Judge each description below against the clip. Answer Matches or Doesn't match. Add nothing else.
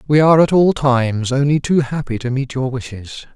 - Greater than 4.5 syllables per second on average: Matches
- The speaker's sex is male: Matches